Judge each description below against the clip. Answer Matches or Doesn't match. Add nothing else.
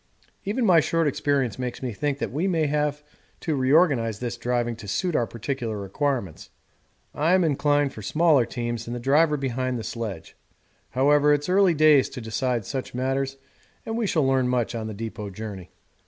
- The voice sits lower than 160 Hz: Matches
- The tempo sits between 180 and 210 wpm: Matches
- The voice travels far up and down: Doesn't match